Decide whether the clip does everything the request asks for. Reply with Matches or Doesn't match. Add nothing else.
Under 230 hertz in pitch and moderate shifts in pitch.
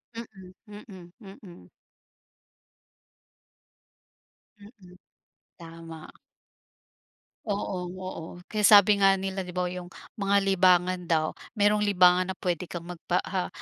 Doesn't match